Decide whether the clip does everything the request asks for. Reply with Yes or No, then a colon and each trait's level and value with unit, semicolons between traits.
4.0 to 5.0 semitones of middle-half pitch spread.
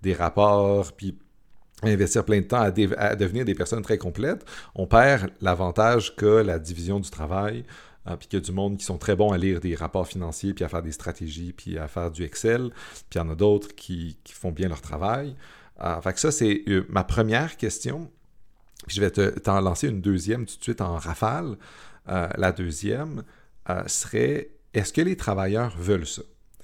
No: average, 3.4 semitones